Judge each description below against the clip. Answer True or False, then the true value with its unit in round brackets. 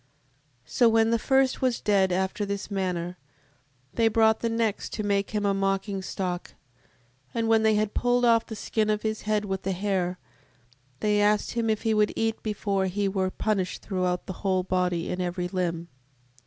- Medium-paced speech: True (190 wpm)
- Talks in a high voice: True (205 Hz)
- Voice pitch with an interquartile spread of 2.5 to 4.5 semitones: True (2.8 semitones)